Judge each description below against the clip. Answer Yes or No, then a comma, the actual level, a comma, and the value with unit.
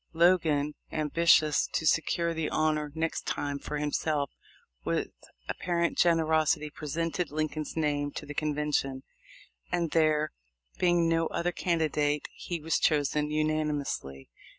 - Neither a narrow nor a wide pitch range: No, narrow, 1.8 semitones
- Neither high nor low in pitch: Yes, medium, 155 Hz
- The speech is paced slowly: Yes, slow, 125 wpm